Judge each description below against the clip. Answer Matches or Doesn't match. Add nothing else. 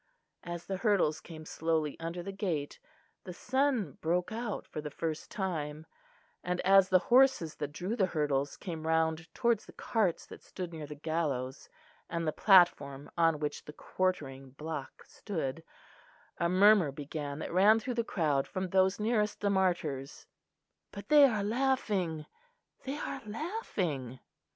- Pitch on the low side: Doesn't match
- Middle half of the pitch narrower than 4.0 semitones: Doesn't match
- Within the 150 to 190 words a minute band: Matches